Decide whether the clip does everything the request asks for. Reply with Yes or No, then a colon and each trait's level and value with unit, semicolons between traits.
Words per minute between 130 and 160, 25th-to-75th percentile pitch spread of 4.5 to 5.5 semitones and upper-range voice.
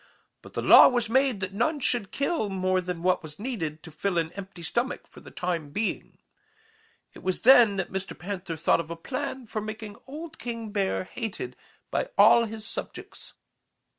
No: average, 180 wpm; average, 4.8 semitones; high, 205 Hz